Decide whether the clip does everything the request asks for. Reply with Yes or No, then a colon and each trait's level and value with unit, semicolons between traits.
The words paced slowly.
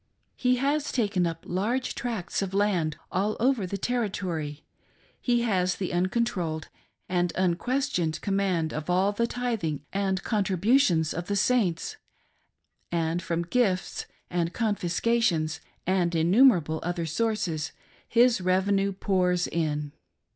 Yes: slow, 125 wpm